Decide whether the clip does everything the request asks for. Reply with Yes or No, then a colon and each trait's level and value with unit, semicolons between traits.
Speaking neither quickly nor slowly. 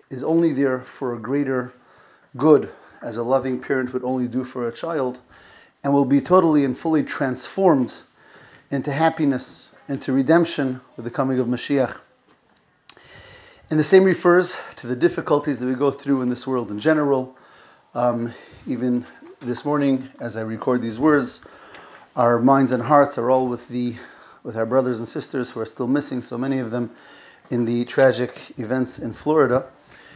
Yes: average, 170 wpm